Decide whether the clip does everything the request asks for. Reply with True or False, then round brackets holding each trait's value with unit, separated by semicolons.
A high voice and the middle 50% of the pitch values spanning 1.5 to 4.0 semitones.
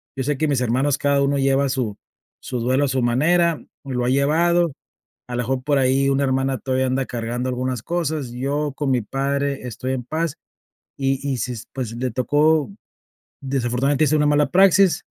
False (135 Hz; 2.4 semitones)